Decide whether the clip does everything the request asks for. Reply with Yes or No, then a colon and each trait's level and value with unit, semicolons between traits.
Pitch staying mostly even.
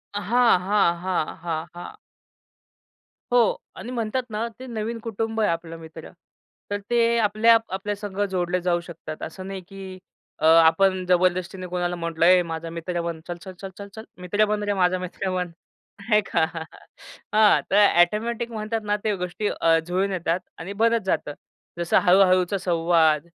No: average, 3.5 semitones